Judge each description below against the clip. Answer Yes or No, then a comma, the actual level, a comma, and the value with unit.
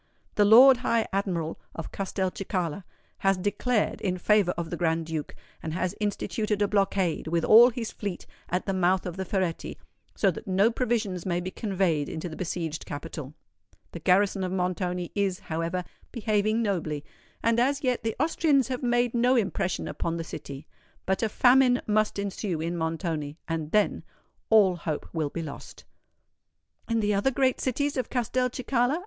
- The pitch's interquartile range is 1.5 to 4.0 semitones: No, average, 4.9 semitones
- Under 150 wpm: No, average, 165 wpm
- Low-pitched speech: No, high, 195 Hz